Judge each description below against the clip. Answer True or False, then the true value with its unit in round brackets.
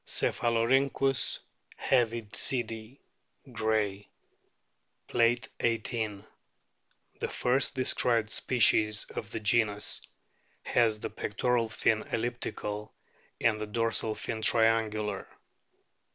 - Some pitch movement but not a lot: False (1.9 semitones)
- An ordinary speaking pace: False (85 wpm)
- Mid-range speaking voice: False (115 Hz)